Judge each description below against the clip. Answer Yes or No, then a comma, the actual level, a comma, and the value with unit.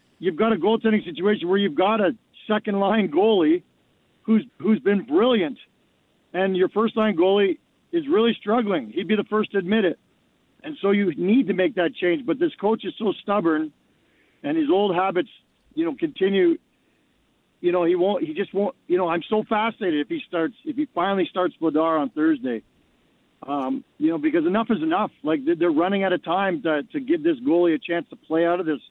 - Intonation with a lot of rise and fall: Yes, wide, 8.1 semitones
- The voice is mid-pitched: No, high, 210 Hz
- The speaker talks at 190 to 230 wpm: Yes, fast, 205 wpm